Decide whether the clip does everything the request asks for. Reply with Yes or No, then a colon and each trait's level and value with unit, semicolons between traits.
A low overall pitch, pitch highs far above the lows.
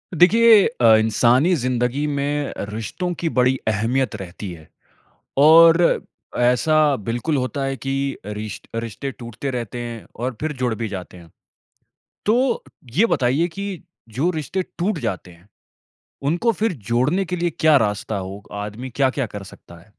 Yes: low, 130 Hz; wide, 6.2 semitones